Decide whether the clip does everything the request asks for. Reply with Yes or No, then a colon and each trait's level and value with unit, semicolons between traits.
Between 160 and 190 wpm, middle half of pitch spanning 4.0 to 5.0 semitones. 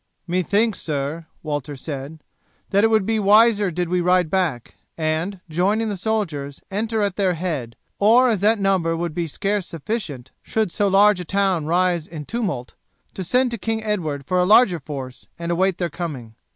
Yes: average, 180 wpm; average, 4.7 semitones